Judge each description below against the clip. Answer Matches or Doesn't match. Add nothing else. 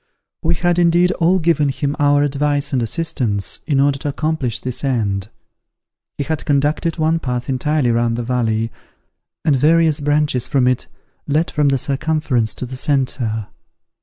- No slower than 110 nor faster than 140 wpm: Doesn't match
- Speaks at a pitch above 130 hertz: Matches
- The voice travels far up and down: Doesn't match